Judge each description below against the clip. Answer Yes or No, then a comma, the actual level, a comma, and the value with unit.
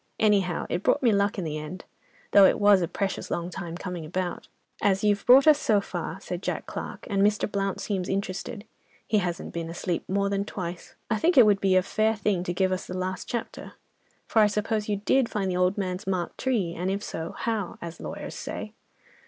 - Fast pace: Yes, fast, 220 wpm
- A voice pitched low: No, high, 195 Hz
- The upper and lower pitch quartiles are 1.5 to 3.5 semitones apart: Yes, narrow, 2.5 semitones